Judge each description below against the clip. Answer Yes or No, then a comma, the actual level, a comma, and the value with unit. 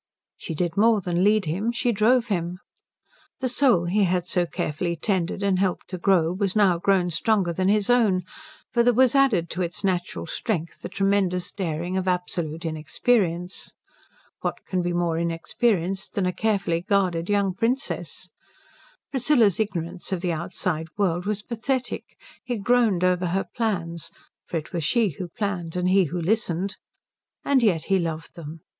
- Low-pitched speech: No, medium, 185 Hz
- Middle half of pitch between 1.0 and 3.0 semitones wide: No, average, 3.6 semitones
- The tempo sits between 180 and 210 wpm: No, average, 165 wpm